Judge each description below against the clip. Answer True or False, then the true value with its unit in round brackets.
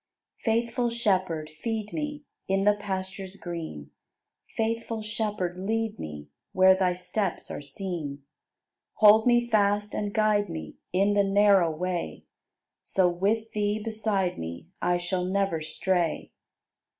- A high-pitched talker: True (195 Hz)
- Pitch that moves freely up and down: False (3.3 semitones)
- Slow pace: True (130 wpm)